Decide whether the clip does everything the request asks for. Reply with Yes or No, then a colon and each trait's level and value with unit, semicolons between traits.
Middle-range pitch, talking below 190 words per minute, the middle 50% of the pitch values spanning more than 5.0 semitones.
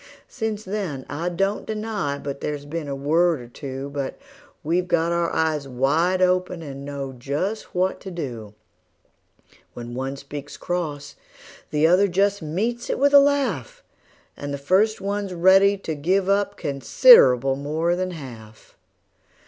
Yes: medium, 165 Hz; average, 150 wpm; wide, 5.6 semitones